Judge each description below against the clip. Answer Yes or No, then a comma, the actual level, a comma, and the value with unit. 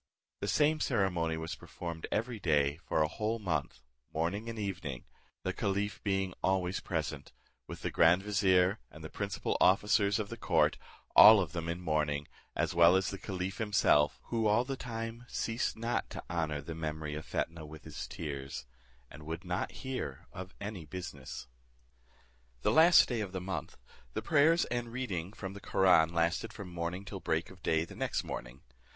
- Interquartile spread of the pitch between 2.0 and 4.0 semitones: No, average, 4.6 semitones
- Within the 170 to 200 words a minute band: Yes, average, 180 wpm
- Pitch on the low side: Yes, very low, 90 Hz